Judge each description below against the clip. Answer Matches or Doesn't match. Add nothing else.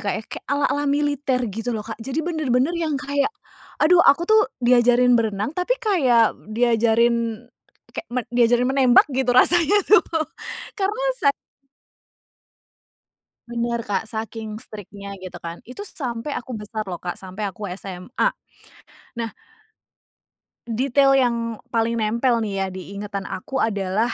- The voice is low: Doesn't match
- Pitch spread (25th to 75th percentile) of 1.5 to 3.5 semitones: Doesn't match